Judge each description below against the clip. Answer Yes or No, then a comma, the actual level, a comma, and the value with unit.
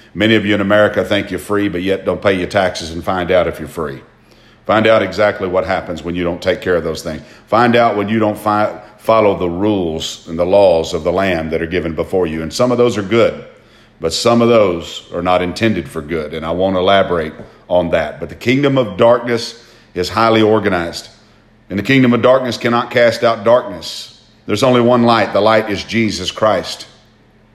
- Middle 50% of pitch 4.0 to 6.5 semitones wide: Yes, average, 4.4 semitones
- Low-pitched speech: Yes, low, 105 Hz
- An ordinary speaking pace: No, fast, 220 wpm